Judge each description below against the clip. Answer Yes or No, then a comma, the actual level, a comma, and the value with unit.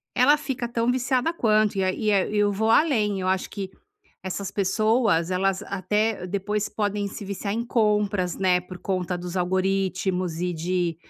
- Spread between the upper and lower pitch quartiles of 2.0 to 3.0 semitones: Yes, narrow, 2.6 semitones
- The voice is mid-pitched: No, high, 200 Hz